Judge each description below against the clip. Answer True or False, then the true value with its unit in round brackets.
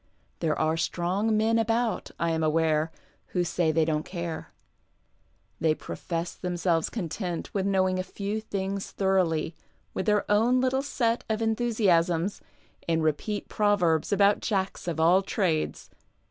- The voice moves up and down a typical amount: True (4.2 semitones)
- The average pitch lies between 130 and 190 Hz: True (185 Hz)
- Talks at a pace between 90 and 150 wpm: True (140 wpm)